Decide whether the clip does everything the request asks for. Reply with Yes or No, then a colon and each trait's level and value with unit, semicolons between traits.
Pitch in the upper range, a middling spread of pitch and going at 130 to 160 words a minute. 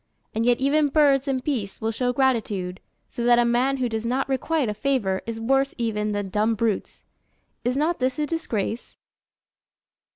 No: high, 245 Hz; average, 3.6 semitones; average, 175 wpm